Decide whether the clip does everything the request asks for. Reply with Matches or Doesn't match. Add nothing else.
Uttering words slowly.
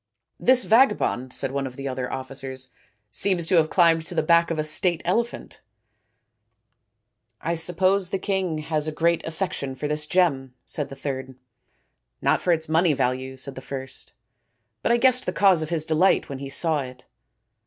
Doesn't match